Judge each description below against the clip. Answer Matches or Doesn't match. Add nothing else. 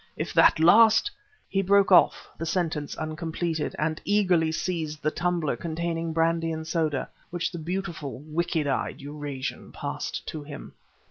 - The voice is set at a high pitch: Doesn't match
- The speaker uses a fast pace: Doesn't match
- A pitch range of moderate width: Doesn't match